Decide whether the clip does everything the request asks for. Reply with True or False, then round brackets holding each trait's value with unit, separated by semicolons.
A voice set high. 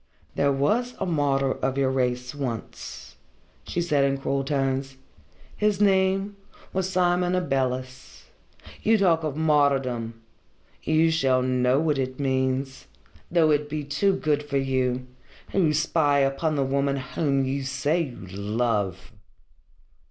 False (140 Hz)